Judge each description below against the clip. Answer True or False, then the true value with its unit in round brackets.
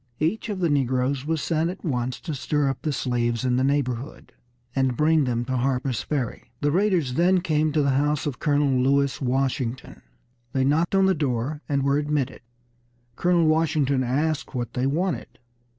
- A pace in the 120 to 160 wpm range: False (180 wpm)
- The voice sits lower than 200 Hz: True (140 Hz)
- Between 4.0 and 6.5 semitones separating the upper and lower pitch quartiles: False (3.3 semitones)